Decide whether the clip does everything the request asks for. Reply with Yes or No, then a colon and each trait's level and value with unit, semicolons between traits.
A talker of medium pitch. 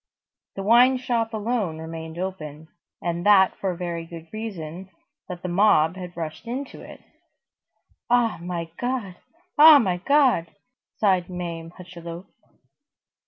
Yes: medium, 180 Hz